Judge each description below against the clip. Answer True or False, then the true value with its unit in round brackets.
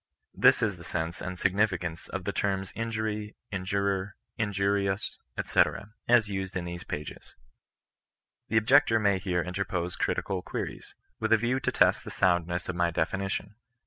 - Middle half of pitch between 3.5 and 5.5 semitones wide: False (2.7 semitones)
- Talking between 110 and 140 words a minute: False (155 wpm)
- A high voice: False (95 Hz)